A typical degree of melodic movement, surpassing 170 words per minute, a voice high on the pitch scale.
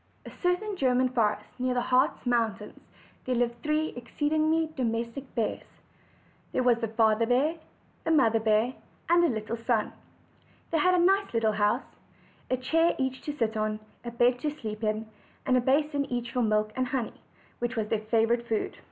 Yes: average, 4.4 semitones; average, 180 wpm; high, 245 Hz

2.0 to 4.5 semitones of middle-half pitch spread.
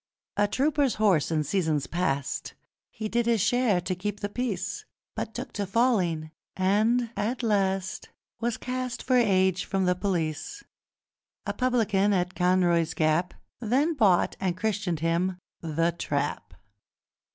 No: average, 4.9 semitones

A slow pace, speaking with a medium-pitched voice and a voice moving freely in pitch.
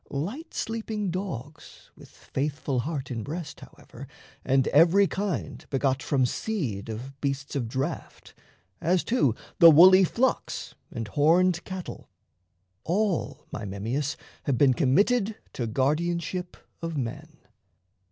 Yes: slow, 125 wpm; medium, 150 Hz; wide, 5.7 semitones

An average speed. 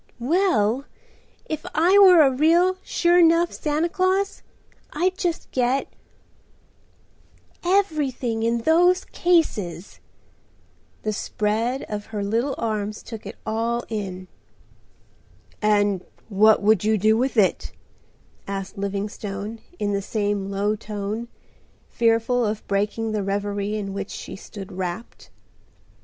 No: slow, 115 wpm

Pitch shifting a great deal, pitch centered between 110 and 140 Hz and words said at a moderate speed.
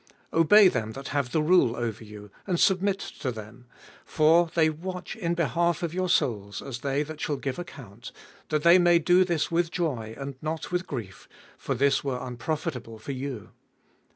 No: wide, 5.7 semitones; medium, 150 Hz; average, 185 wpm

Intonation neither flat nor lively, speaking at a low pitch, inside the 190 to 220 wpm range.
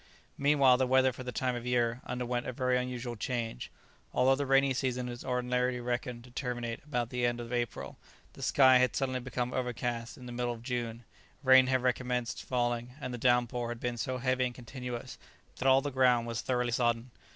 No: narrow, 1.1 semitones; low, 125 Hz; average, 200 wpm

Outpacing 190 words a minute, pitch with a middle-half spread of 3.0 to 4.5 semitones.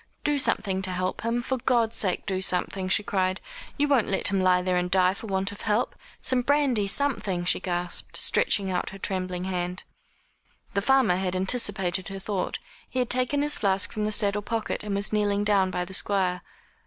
Yes: average, 200 wpm; average, 3.3 semitones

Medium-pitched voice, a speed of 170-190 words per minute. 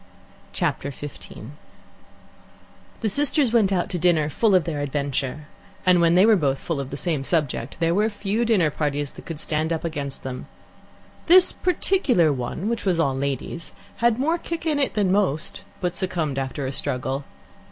Yes: medium, 165 Hz; average, 175 wpm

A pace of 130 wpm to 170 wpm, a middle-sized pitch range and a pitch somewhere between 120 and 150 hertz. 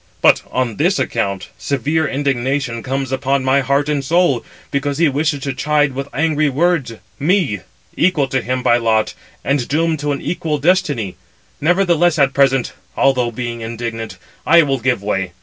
Yes: average, 165 wpm; average, 3.6 semitones; medium, 140 Hz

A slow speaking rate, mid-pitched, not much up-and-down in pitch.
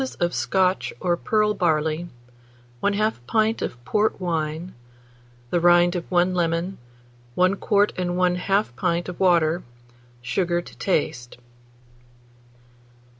Yes: slow, 115 wpm; medium, 175 Hz; narrow, 2.2 semitones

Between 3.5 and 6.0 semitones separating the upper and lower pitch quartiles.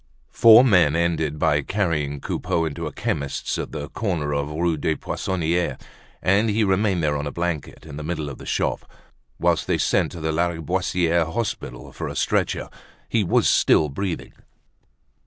Yes: average, 3.8 semitones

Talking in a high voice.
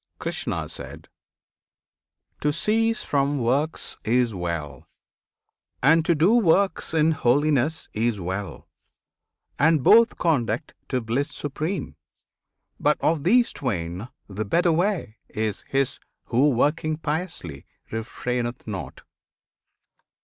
No: medium, 140 Hz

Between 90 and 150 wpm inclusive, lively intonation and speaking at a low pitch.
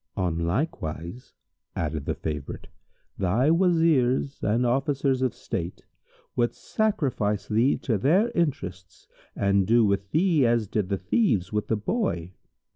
Yes: slow, 135 wpm; wide, 7.3 semitones; low, 115 Hz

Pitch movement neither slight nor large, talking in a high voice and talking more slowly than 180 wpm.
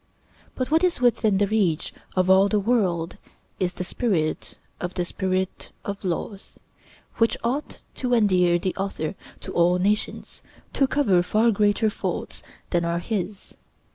Yes: average, 3.7 semitones; high, 195 Hz; average, 150 wpm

